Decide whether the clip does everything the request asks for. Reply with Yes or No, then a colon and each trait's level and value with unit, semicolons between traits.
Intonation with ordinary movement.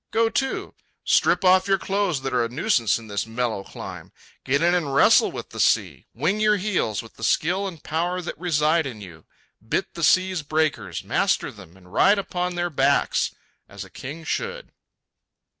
No: wide, 7.0 semitones